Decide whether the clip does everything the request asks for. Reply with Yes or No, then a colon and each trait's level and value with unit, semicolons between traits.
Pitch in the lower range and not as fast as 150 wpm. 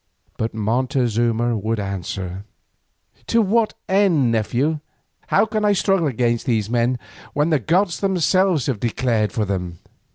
Yes: low, 125 Hz; slow, 135 wpm